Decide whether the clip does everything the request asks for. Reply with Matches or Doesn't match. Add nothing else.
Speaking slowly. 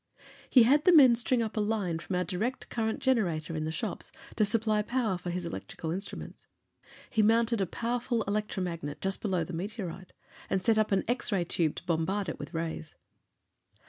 Doesn't match